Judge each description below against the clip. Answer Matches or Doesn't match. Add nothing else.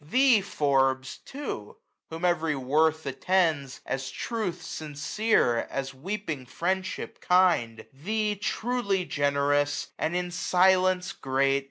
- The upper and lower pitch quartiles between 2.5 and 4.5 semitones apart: Doesn't match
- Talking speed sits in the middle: Doesn't match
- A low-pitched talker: Doesn't match